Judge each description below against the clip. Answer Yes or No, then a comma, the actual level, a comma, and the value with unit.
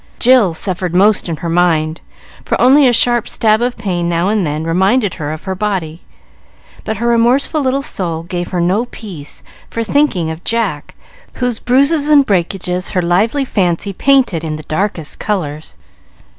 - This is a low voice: No, high, 190 Hz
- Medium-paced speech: Yes, average, 170 wpm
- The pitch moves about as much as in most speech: No, wide, 5.9 semitones